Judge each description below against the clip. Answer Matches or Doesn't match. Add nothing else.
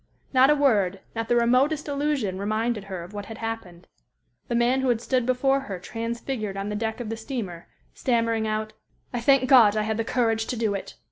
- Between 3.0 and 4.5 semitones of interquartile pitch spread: Matches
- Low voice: Doesn't match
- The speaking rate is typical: Doesn't match